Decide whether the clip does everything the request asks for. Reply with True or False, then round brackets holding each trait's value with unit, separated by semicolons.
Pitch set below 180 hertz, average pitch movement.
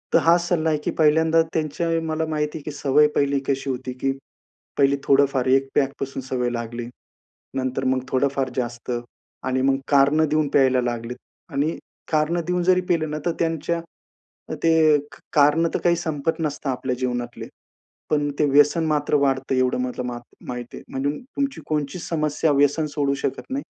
True (140 Hz; 3.3 semitones)